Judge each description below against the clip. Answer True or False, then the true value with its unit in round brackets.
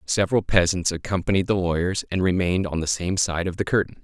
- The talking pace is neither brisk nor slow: False (210 wpm)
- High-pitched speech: False (90 Hz)